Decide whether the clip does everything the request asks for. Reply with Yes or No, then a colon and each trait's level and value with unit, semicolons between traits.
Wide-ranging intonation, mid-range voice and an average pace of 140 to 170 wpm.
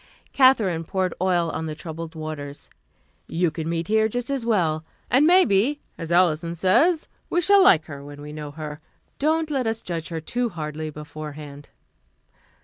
Yes: wide, 7.0 semitones; medium, 170 Hz; average, 165 wpm